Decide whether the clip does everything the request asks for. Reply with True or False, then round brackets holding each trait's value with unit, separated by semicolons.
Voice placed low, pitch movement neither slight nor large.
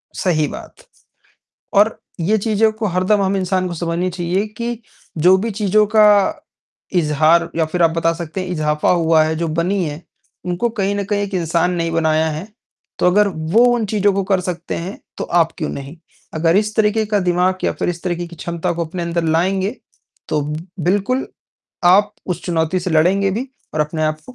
False (180 Hz; 3.4 semitones)